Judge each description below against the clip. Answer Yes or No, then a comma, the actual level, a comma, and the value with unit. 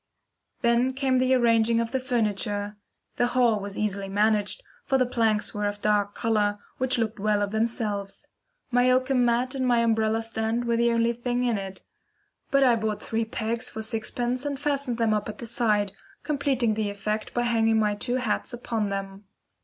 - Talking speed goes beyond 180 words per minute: Yes, average, 190 wpm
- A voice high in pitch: Yes, high, 230 Hz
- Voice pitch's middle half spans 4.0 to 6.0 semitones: No, average, 2.7 semitones